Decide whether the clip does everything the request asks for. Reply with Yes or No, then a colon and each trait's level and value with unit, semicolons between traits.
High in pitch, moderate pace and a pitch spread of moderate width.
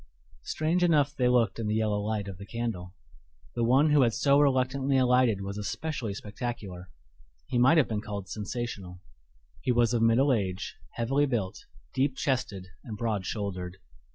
No: low, 115 Hz; average, 165 wpm; average, 4.5 semitones